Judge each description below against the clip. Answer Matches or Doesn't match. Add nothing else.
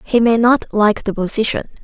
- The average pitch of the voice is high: Matches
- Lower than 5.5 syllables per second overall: Matches